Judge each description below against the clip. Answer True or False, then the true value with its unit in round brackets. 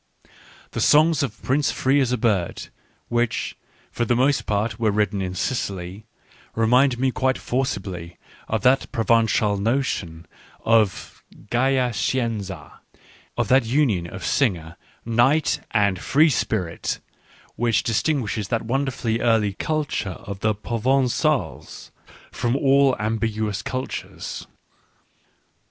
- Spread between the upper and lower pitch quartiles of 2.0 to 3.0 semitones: False (4.3 semitones)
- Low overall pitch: True (115 Hz)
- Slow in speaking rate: True (120 wpm)